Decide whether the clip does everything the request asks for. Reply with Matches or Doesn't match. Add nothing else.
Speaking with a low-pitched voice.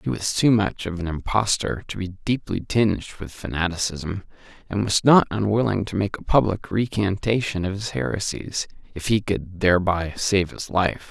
Matches